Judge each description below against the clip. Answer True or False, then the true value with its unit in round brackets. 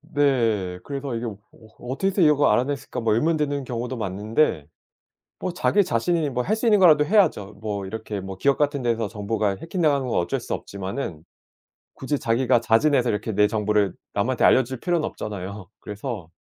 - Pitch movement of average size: False (5.8 semitones)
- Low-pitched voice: True (120 Hz)